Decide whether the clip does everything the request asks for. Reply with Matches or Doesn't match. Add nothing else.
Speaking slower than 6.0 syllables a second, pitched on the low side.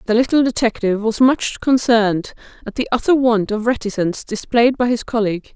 Doesn't match